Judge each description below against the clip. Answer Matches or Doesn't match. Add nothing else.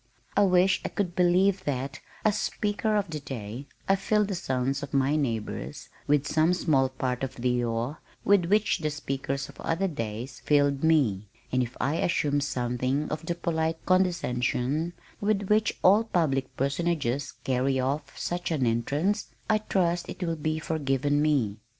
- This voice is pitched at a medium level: Matches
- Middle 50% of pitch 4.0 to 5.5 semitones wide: Matches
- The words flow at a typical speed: Matches